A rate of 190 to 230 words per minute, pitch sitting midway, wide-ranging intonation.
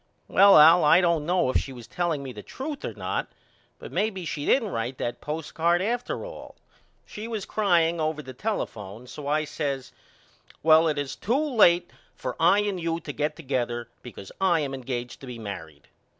Yes: average, 195 wpm; medium, 155 Hz; wide, 5.8 semitones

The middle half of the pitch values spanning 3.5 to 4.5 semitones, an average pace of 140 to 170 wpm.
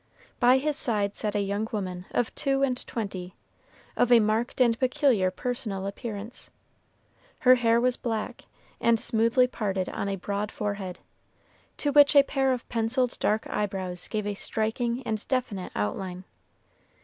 Yes: average, 3.8 semitones; average, 150 wpm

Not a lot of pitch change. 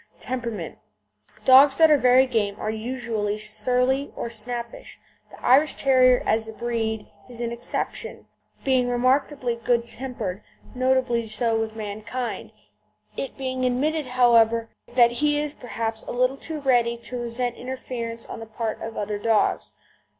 Yes: narrow, 2.3 semitones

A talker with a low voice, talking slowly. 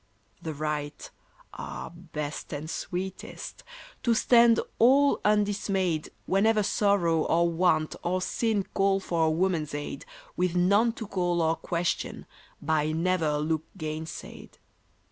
No: medium, 175 Hz; slow, 125 wpm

